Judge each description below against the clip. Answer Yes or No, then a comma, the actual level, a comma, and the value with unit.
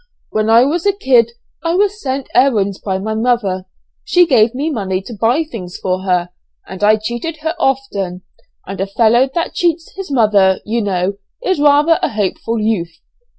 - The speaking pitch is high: Yes, high, 230 Hz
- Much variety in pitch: Yes, wide, 6.6 semitones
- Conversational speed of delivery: Yes, average, 180 wpm